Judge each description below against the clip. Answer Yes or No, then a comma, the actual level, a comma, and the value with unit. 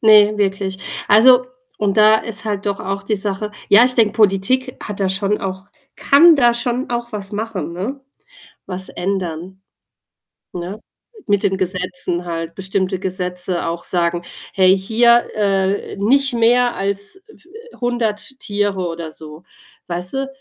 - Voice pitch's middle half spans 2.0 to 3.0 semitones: No, average, 3.4 semitones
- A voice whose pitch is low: No, high, 200 Hz